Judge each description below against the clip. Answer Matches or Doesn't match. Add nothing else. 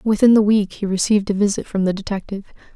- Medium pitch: Doesn't match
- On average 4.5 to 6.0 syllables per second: Doesn't match